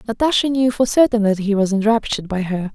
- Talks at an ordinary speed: No, fast, 220 wpm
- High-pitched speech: Yes, high, 215 Hz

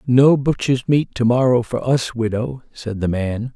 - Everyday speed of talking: Yes, average, 185 wpm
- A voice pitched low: Yes, low, 120 Hz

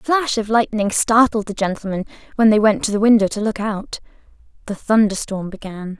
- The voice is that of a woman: Yes, female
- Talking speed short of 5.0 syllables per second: No, 5.5 syllables/s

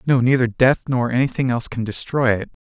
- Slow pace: No, fast, 205 wpm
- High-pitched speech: No, low, 125 Hz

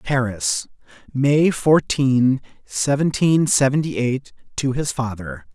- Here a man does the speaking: Yes, male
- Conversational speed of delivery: No, slow, 95 wpm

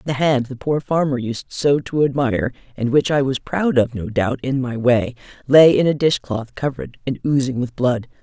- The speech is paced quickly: Yes, fast, 210 wpm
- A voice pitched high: No, low, 130 Hz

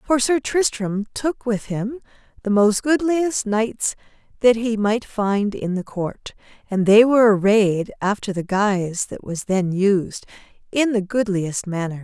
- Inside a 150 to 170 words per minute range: Yes, average, 160 wpm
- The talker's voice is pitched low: No, high, 215 Hz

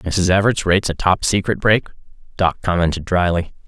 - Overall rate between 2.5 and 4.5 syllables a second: No, 5.4 syllables/s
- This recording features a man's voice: Yes, male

